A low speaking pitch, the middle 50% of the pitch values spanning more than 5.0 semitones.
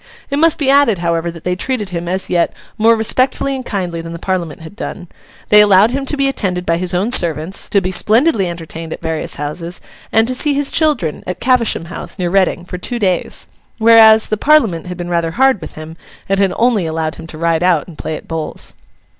No: medium, 185 Hz; wide, 5.5 semitones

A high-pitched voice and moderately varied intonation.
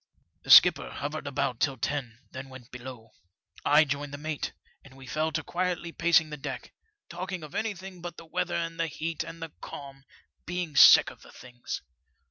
No: medium, 155 Hz; average, 3.6 semitones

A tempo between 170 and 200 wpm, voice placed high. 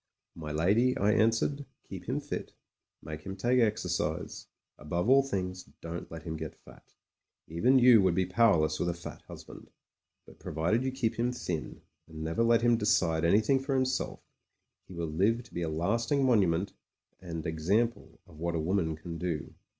No: average, 180 wpm; very low, 95 Hz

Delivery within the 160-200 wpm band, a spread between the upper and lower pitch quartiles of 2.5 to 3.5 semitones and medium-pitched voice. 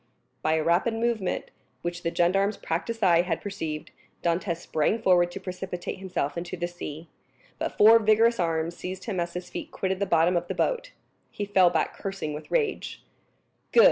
Yes: average, 180 wpm; average, 3.1 semitones; medium, 180 Hz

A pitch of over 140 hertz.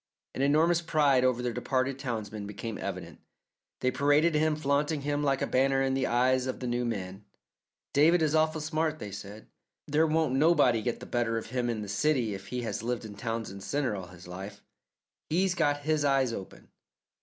No: low, 130 Hz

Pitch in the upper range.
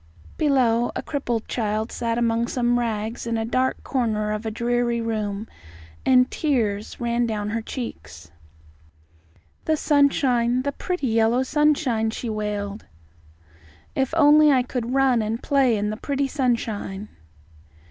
Yes: high, 235 Hz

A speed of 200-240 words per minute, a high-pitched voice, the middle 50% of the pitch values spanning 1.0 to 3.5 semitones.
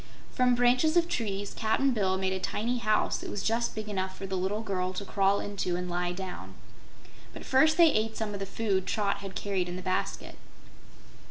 Yes: fast, 205 wpm; high, 200 Hz; average, 3.2 semitones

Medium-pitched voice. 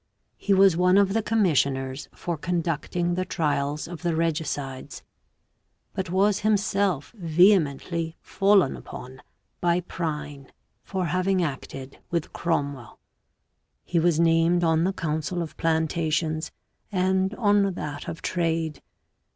Yes: medium, 170 Hz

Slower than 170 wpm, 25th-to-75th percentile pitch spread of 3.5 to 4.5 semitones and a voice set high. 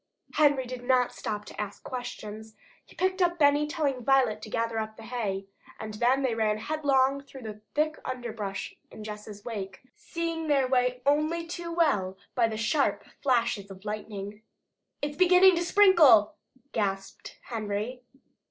No: average, 155 wpm; wide, 5.6 semitones; high, 245 Hz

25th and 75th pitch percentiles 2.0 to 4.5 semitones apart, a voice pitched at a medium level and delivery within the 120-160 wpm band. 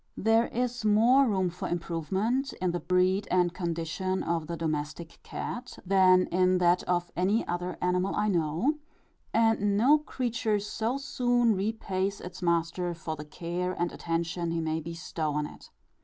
Yes: average, 4.1 semitones; medium, 180 Hz; average, 155 wpm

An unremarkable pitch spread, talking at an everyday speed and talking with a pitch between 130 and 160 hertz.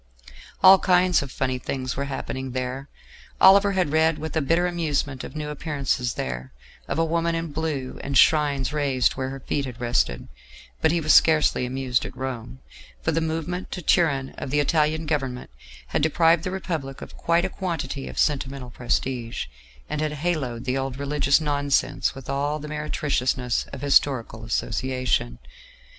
Yes: average, 3.5 semitones; average, 170 wpm; medium, 140 Hz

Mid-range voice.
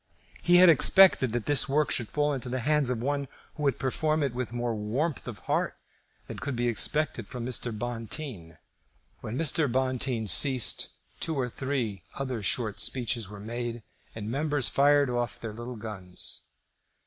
No: low, 125 Hz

